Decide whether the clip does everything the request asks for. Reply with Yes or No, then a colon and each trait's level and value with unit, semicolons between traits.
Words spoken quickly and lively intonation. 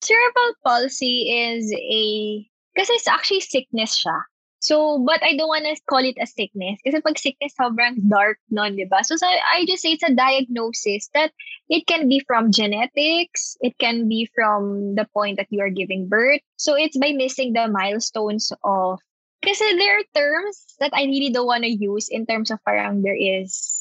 No: average, 185 wpm; wide, 6.3 semitones